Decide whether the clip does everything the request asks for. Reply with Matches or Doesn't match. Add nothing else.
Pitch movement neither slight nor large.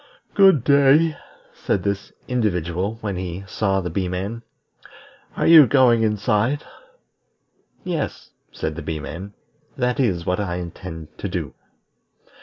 Doesn't match